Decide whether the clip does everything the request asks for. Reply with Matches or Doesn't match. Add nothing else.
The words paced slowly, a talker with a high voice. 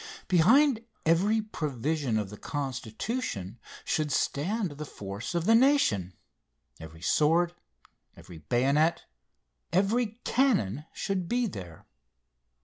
Doesn't match